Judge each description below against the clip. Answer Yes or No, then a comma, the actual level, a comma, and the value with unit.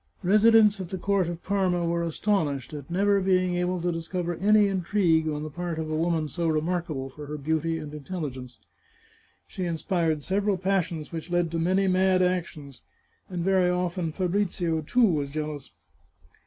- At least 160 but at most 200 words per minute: Yes, average, 170 wpm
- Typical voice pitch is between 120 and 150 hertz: No, medium, 175 Hz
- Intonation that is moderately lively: Yes, average, 3.0 semitones